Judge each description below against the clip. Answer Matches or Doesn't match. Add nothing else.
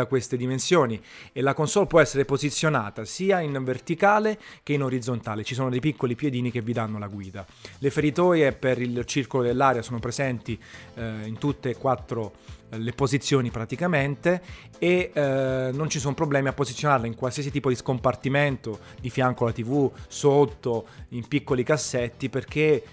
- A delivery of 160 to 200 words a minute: Matches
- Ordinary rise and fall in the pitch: Matches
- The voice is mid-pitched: Doesn't match